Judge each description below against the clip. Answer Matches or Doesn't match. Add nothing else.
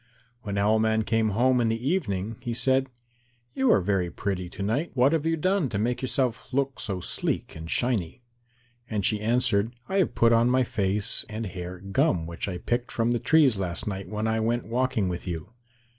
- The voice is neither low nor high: Doesn't match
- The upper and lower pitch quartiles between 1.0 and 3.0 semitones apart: Doesn't match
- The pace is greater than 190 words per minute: Matches